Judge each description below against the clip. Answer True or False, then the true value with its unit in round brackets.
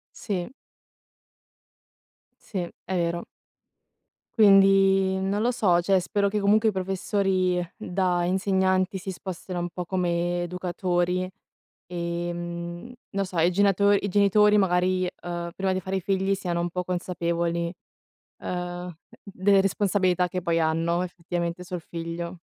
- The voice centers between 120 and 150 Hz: False (180 Hz)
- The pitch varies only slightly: True (1.9 semitones)